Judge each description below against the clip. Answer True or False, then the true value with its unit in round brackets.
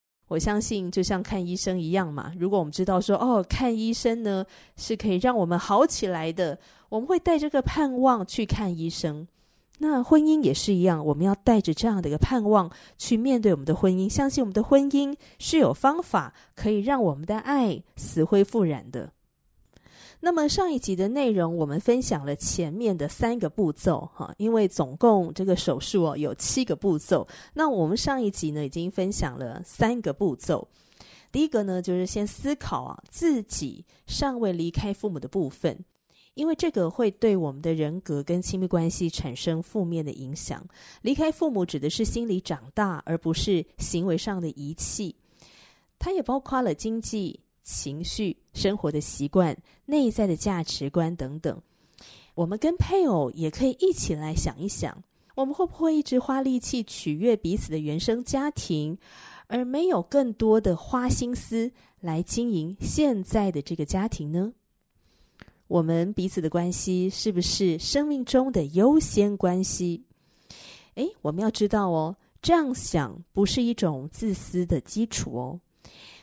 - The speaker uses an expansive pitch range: True (6.1 semitones)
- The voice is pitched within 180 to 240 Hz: True (190 Hz)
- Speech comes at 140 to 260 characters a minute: True (255 characters per minute)